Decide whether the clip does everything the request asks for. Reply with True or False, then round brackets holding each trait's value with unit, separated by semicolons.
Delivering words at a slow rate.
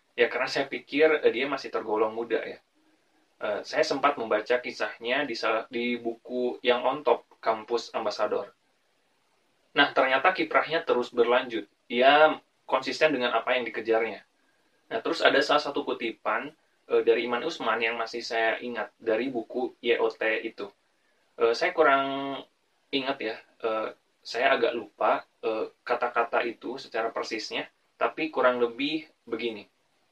False (140 wpm)